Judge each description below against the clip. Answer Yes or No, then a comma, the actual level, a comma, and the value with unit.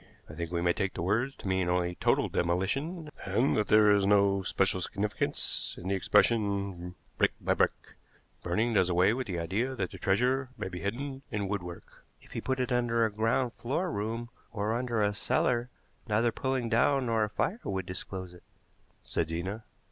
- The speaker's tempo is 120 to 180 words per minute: No, average, 190 wpm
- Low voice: Yes, low, 105 Hz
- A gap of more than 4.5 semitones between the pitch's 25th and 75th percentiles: No, average, 4.2 semitones